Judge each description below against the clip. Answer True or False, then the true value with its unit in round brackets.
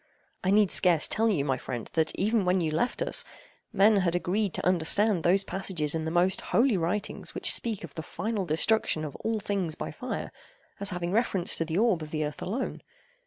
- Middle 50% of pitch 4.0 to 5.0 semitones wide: True (4.4 semitones)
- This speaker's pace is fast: True (210 wpm)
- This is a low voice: False (185 Hz)